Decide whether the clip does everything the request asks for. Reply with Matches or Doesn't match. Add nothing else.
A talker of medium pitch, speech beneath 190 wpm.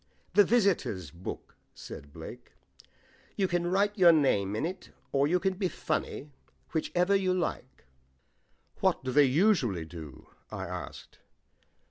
Matches